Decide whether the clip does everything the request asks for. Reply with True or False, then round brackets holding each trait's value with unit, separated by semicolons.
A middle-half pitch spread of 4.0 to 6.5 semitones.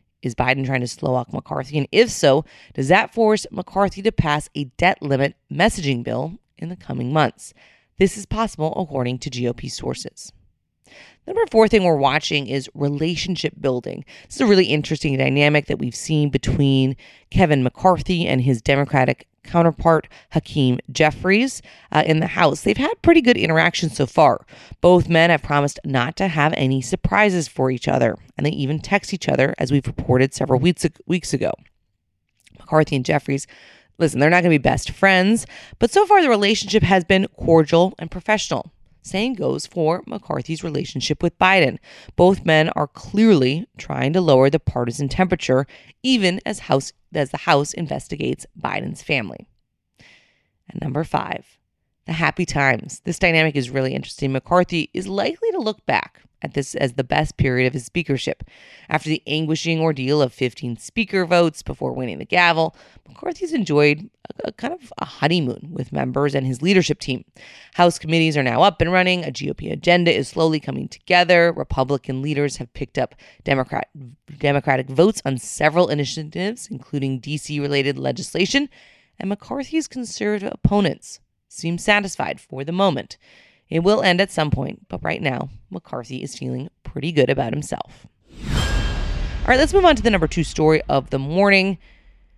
True (5.2 semitones)